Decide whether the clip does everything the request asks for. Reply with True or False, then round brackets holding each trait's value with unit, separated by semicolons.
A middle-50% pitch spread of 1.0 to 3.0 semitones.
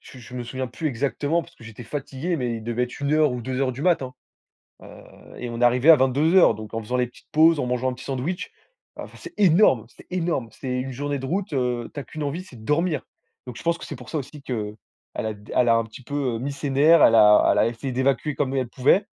False (3.8 semitones)